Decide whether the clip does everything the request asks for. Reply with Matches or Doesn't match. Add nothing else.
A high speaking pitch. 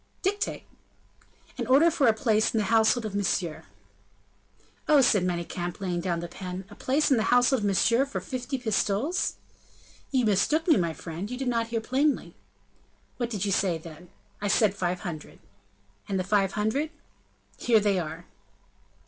Matches